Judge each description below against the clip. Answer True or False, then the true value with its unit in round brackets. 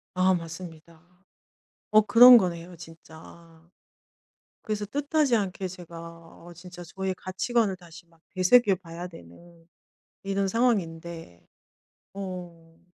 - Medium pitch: True (175 Hz)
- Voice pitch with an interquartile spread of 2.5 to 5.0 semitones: True (2.9 semitones)